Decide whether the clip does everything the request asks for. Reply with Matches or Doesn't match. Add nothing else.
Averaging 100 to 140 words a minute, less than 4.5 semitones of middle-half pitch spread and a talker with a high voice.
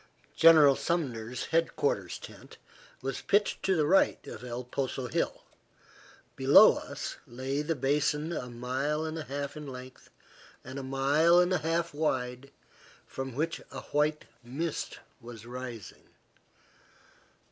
Doesn't match